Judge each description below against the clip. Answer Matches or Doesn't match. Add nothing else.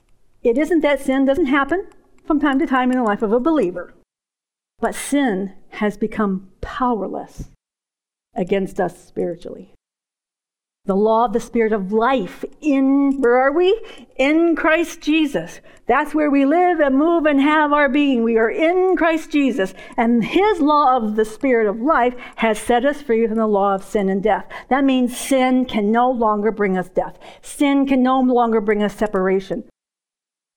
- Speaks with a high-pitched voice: Matches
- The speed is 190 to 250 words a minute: Doesn't match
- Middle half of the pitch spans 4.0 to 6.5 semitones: Matches